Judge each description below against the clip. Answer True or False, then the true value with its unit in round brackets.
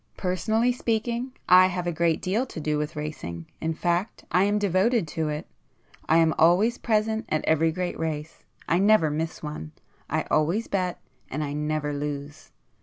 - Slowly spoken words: False (165 wpm)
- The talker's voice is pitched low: False (170 Hz)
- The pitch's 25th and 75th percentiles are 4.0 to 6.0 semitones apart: True (5.1 semitones)